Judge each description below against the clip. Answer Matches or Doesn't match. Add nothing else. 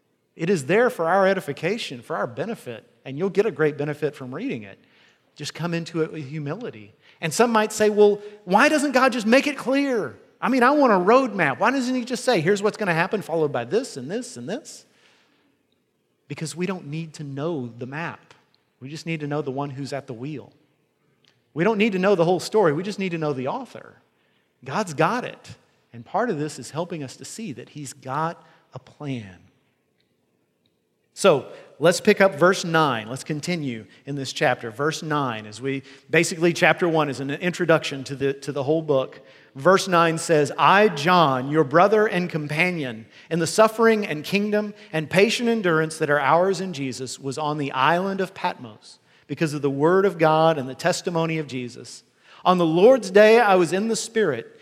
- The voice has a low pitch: Doesn't match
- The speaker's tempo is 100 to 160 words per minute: Doesn't match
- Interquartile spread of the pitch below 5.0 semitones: Doesn't match